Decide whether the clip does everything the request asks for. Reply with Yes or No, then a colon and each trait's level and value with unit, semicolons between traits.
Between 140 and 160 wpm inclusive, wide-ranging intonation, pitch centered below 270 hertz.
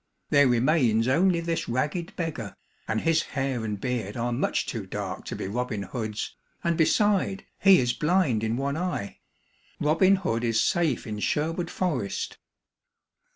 Yes: average, 155 wpm; wide, 6.6 semitones; low, 135 Hz